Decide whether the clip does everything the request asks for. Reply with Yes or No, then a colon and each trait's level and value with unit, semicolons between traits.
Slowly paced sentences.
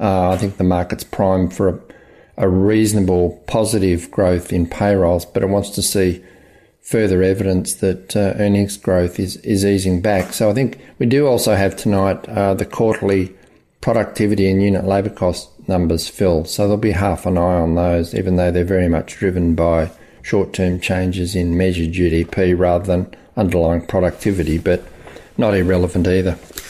No: average, 170 wpm